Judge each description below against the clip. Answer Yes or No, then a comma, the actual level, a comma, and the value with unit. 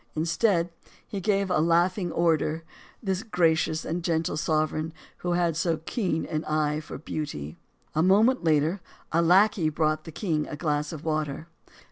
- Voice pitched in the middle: Yes, medium, 165 Hz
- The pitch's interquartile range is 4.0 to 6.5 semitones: No, narrow, 2.4 semitones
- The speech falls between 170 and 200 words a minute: No, average, 155 wpm